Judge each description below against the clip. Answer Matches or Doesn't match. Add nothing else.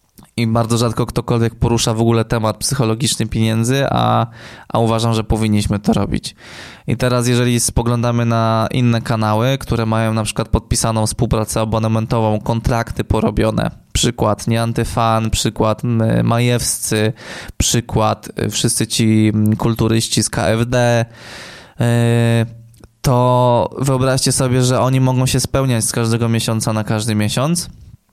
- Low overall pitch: Matches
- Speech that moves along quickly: Doesn't match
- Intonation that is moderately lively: Doesn't match